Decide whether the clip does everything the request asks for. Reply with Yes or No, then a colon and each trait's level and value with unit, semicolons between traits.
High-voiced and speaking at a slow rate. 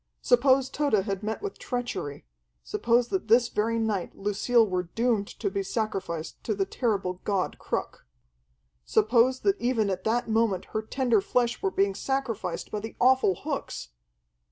No: high, 220 Hz; average, 155 wpm